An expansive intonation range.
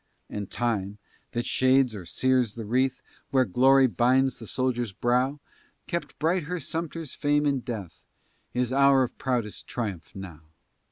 No: average, 3.3 semitones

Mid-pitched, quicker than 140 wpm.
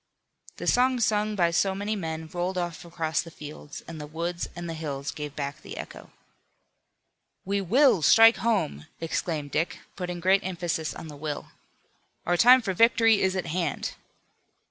Yes: medium, 175 Hz; average, 165 wpm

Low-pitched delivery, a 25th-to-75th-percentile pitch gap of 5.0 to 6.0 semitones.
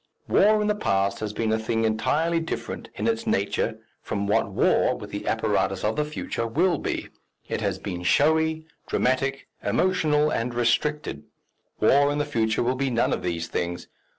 Yes: low, 125 Hz; wide, 5.6 semitones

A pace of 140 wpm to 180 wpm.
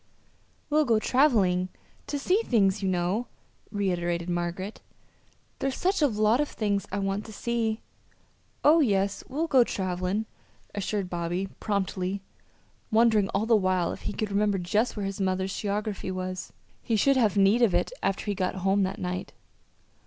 Yes: average, 160 wpm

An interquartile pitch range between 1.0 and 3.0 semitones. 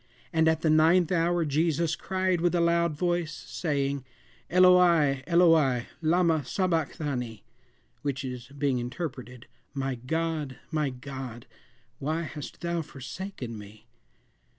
No: average, 4.2 semitones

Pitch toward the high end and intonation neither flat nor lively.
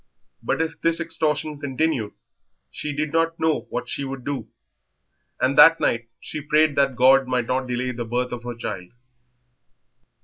No: low, 135 Hz; average, 3.8 semitones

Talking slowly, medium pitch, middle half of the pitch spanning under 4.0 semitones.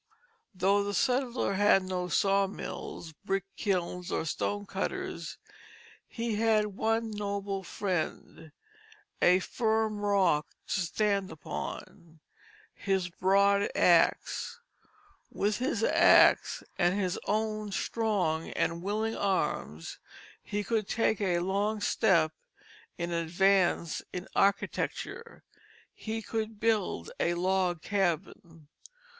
No: slow, 105 wpm; high, 195 Hz; average, 3.2 semitones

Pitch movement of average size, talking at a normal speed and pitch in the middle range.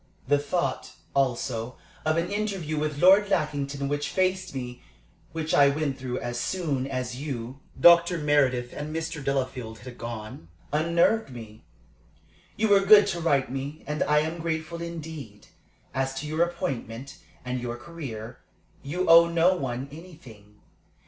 Yes: average, 4.9 semitones; average, 150 wpm; medium, 145 Hz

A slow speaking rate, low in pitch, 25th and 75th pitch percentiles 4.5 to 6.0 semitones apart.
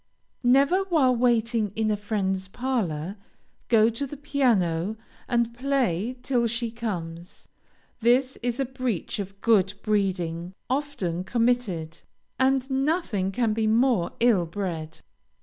No: slow, 125 wpm; high, 225 Hz; average, 5.0 semitones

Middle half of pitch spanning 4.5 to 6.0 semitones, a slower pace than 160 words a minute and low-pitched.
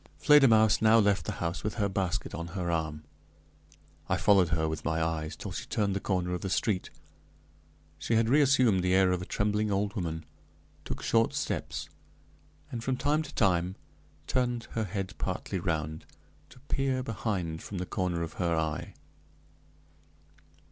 No: average, 4.8 semitones; average, 165 wpm; very low, 95 Hz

